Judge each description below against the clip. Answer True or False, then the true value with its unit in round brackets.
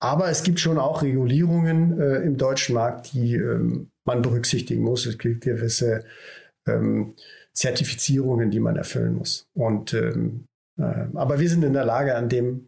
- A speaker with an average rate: True (165 wpm)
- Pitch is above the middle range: False (130 Hz)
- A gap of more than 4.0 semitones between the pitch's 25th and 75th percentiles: True (4.7 semitones)